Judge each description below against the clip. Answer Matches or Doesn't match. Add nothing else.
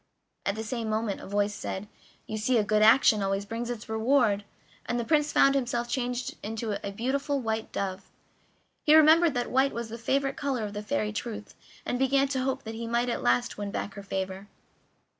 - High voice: Matches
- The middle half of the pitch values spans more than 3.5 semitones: Matches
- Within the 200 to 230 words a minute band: Matches